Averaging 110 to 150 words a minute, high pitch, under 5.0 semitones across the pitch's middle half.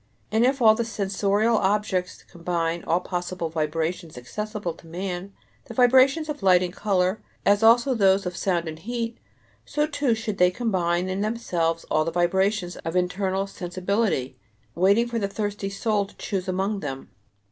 No: average, 165 wpm; high, 195 Hz; average, 3.6 semitones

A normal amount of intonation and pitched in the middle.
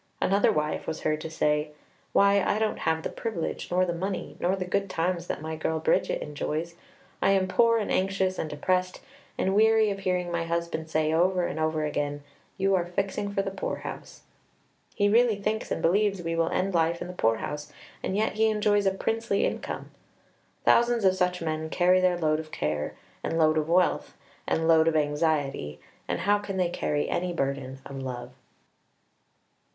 Yes: average, 3.8 semitones; medium, 175 Hz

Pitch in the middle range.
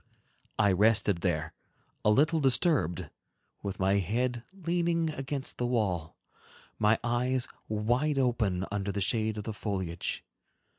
No: low, 110 Hz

